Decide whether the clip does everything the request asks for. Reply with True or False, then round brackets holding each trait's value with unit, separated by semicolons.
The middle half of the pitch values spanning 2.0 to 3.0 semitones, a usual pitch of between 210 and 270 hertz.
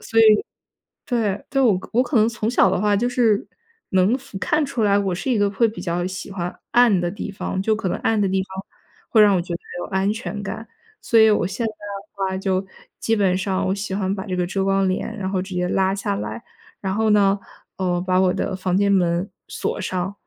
False (2.4 semitones; 195 Hz)